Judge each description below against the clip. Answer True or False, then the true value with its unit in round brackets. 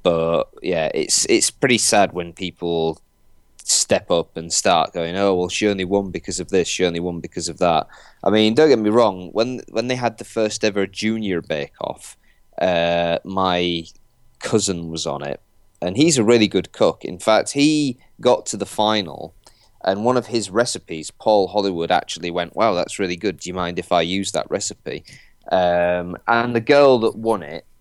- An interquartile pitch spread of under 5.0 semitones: True (4.3 semitones)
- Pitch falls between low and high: False (95 Hz)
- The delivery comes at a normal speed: True (195 wpm)